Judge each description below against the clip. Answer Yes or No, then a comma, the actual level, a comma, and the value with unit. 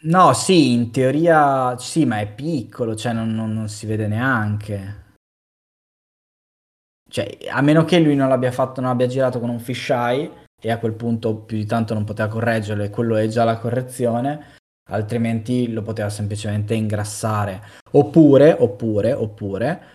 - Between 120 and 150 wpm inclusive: No, average, 160 wpm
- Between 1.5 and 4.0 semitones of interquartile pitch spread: Yes, average, 3.2 semitones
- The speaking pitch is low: Yes, low, 115 Hz